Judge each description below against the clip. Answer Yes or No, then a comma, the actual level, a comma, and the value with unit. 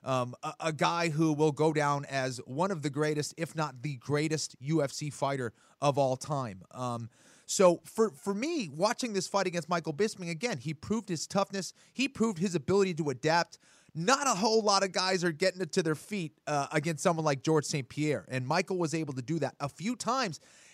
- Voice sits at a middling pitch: Yes, medium, 160 Hz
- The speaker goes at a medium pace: No, fast, 210 wpm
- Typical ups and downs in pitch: Yes, average, 4.6 semitones